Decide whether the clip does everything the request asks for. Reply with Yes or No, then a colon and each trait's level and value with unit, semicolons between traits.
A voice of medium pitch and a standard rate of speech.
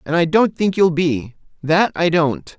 No: medium, 165 Hz; fast, 210 wpm